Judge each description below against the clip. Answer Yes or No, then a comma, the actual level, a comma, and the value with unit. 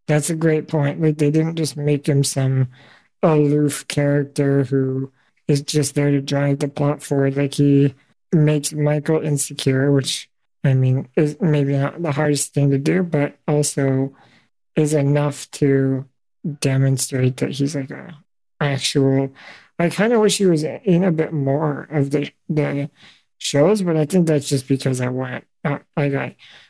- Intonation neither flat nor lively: No, narrow, 1.9 semitones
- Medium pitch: Yes, medium, 145 Hz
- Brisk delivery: No, average, 165 wpm